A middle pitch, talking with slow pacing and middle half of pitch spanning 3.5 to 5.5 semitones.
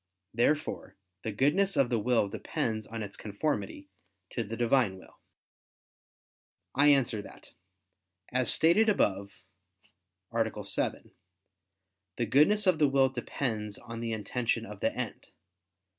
No: low, 120 Hz; slow, 130 wpm; average, 4.6 semitones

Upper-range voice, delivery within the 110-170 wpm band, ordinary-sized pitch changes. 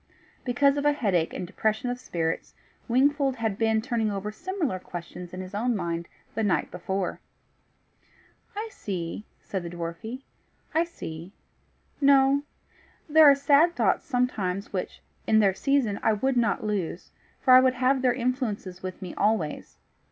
No: high, 220 Hz; average, 155 wpm; wide, 6.1 semitones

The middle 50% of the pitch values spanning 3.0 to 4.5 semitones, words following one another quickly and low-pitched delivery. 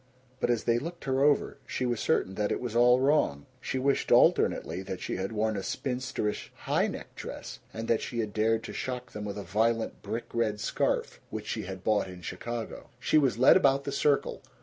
Yes: average, 3.7 semitones; fast, 215 wpm; low, 115 Hz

